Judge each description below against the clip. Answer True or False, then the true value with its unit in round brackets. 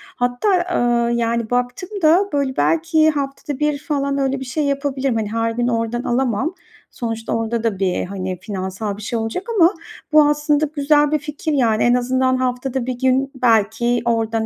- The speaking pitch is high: True (250 Hz)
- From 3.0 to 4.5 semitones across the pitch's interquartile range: True (4.1 semitones)